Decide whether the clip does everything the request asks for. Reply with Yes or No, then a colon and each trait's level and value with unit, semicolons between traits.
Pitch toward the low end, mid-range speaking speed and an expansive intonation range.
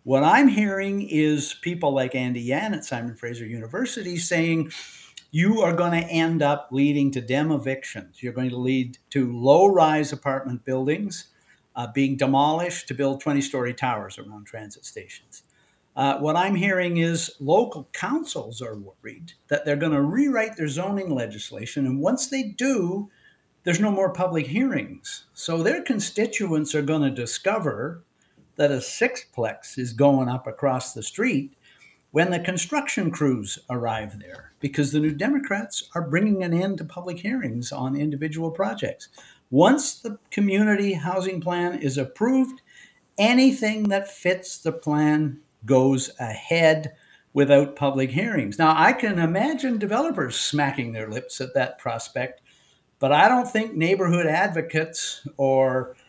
No: medium, 155 Hz; average, 150 wpm; wide, 6.3 semitones